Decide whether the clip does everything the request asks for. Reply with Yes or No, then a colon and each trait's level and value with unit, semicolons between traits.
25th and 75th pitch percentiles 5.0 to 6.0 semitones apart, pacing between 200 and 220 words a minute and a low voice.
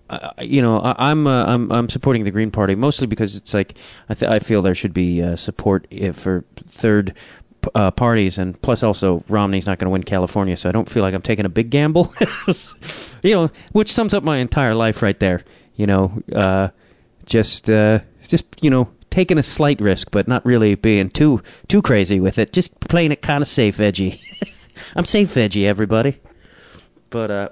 Yes: average, 5.3 semitones; fast, 205 wpm; low, 110 Hz